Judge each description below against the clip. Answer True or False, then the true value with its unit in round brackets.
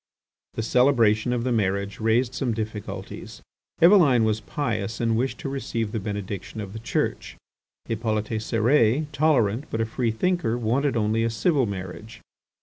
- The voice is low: True (115 Hz)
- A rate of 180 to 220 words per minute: False (150 wpm)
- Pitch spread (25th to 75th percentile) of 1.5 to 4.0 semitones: True (2.8 semitones)